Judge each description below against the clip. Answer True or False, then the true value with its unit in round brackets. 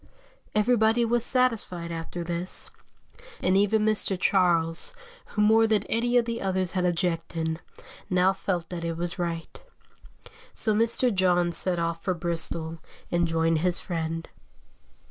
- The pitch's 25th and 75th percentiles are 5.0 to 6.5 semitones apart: False (4.2 semitones)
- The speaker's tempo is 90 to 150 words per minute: True (140 wpm)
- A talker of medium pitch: True (180 Hz)